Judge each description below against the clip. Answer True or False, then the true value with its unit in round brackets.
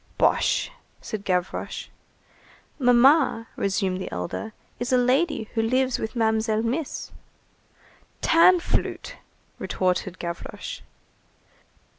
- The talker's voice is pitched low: False (230 Hz)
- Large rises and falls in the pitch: False (4.8 semitones)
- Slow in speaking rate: True (90 wpm)